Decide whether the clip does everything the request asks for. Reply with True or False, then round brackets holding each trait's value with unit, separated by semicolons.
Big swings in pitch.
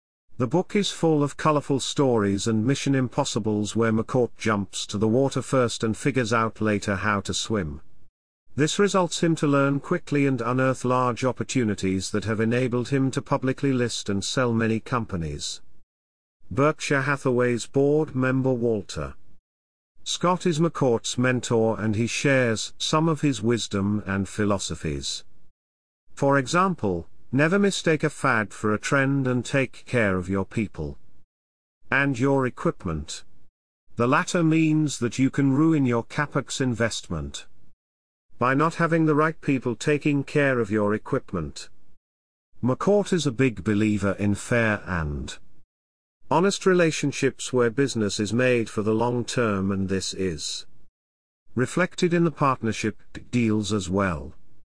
True (6.0 semitones)